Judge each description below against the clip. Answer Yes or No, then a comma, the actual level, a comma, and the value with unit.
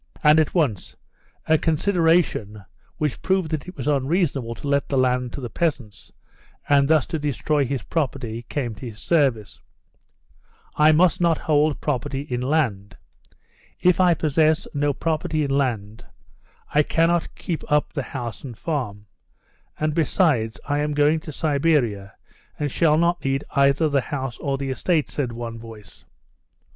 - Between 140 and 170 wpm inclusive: Yes, average, 155 wpm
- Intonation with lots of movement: No, average, 4.1 semitones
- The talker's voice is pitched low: No, medium, 145 Hz